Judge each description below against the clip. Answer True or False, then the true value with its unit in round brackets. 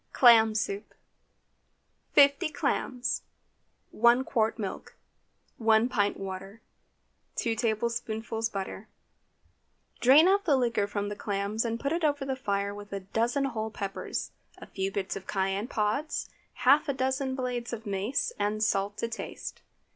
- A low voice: False (225 Hz)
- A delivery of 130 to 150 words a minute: True (140 wpm)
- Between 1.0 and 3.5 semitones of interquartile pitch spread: False (4.1 semitones)